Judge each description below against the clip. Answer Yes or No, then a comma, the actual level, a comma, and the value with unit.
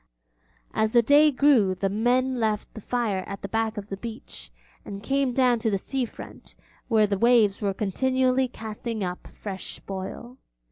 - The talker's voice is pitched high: Yes, high, 225 Hz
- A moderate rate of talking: Yes, average, 175 wpm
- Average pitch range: Yes, average, 4.0 semitones